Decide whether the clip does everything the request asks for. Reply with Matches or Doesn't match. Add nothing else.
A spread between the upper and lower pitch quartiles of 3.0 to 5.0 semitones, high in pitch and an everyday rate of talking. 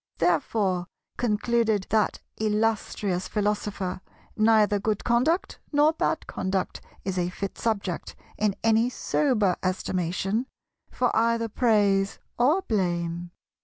Doesn't match